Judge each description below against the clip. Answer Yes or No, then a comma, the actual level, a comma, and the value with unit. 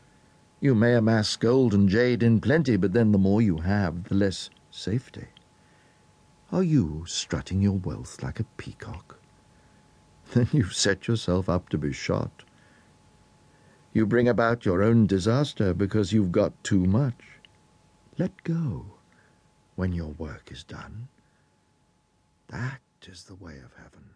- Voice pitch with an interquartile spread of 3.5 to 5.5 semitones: Yes, average, 4.5 semitones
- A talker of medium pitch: No, low, 105 Hz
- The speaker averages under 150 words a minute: Yes, average, 140 wpm